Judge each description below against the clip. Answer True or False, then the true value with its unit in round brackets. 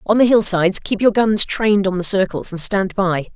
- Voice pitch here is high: True (200 Hz)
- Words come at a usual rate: False (235 wpm)